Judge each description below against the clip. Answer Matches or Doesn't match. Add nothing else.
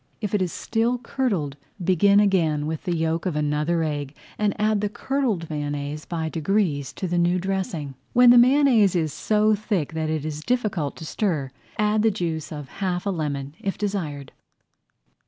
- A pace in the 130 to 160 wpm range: Doesn't match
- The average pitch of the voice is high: Doesn't match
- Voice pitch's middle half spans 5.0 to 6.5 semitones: Matches